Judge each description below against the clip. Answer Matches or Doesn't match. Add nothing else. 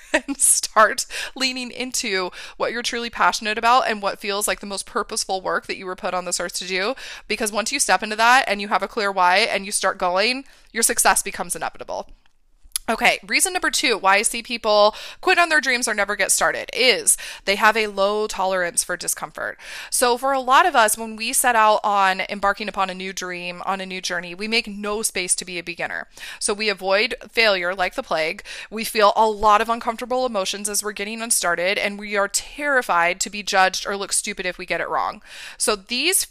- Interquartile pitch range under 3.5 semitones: Doesn't match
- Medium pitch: Doesn't match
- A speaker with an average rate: Doesn't match